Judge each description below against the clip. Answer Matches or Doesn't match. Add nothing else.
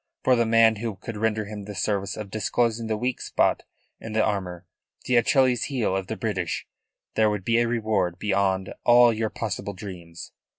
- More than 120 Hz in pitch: Doesn't match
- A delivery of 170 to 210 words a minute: Matches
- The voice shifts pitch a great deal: Doesn't match